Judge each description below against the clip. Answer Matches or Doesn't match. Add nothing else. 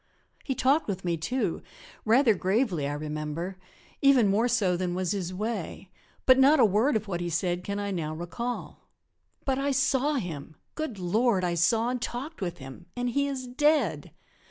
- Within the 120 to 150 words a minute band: Doesn't match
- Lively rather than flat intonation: Matches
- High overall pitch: Matches